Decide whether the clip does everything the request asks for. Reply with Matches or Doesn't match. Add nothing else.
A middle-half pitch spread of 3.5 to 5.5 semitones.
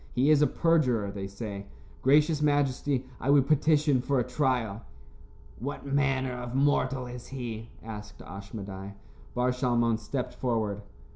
Matches